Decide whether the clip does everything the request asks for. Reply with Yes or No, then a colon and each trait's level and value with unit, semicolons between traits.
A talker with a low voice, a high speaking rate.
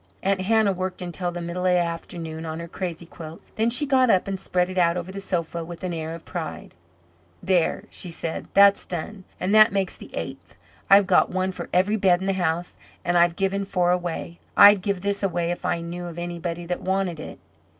No: medium, 180 Hz; fast, 220 wpm